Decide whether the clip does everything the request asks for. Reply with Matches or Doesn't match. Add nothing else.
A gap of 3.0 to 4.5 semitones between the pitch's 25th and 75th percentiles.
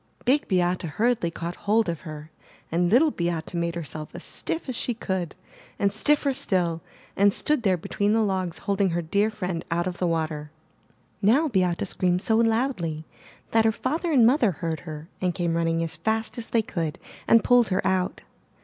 Doesn't match